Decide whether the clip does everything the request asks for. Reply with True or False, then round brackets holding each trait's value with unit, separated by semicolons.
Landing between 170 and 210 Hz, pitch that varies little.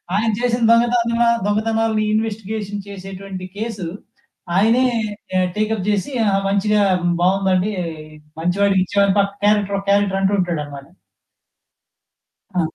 True (200 Hz; 2.3 semitones)